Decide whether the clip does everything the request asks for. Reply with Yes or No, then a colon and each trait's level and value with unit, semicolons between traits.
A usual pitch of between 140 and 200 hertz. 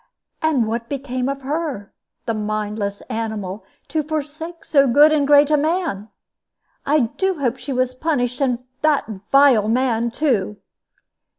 No: very high, 260 Hz